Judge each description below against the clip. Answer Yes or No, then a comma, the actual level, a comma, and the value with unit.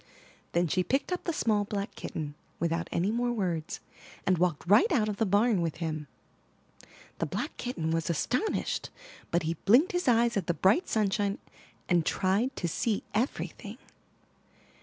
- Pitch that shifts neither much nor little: No, wide, 5.7 semitones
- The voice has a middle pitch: No, high, 200 Hz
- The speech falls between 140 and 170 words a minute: Yes, average, 165 wpm